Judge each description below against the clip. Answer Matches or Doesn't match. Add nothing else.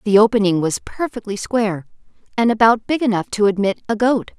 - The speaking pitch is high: Matches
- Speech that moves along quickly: Doesn't match